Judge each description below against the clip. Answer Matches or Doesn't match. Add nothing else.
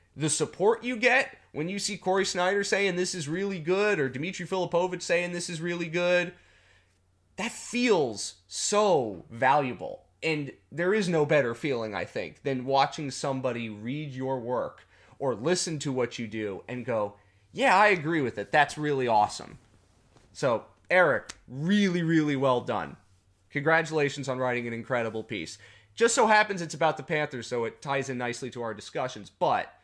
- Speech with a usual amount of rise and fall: Doesn't match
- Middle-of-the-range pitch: Matches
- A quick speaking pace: Doesn't match